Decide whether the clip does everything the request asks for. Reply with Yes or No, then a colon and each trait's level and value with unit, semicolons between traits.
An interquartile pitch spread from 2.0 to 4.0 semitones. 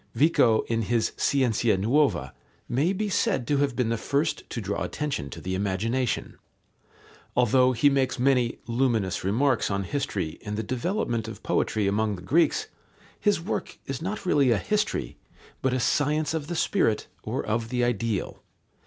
No: average, 4.7 semitones